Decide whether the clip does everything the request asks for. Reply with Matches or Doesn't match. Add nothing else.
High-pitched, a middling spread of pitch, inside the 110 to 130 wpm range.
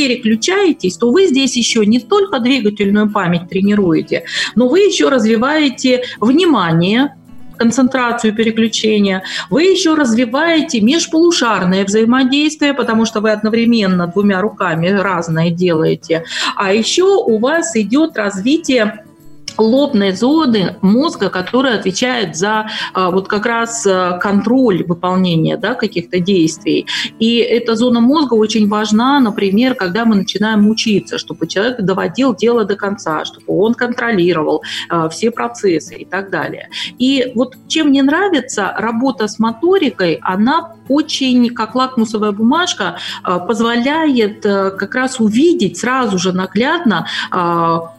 Matches